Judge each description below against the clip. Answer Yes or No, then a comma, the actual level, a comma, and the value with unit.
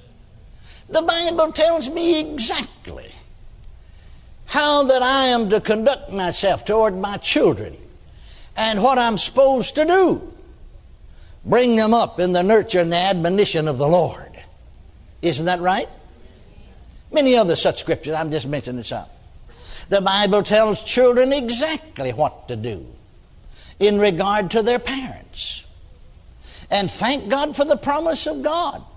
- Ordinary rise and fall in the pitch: No, wide, 8.1 semitones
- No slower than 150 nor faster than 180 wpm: No, slow, 135 wpm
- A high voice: Yes, high, 220 Hz